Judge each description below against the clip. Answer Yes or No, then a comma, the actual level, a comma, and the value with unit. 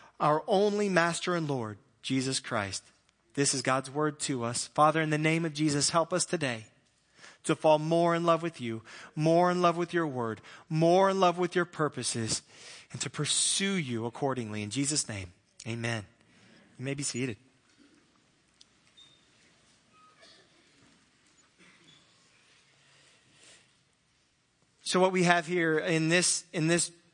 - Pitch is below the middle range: No, medium, 150 Hz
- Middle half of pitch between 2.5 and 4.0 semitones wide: No, average, 5.3 semitones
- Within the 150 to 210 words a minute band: No, average, 140 wpm